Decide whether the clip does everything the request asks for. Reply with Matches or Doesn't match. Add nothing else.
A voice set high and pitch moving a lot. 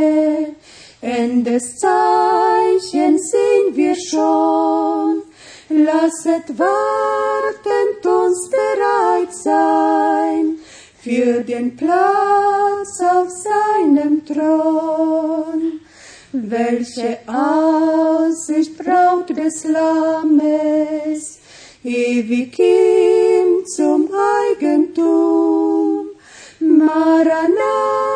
Matches